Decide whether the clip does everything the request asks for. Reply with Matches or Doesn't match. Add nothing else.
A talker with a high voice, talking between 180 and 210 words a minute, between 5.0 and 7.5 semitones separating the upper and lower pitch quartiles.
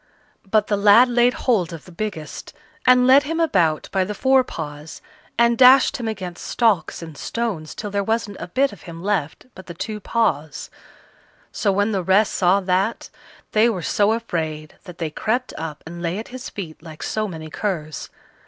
Matches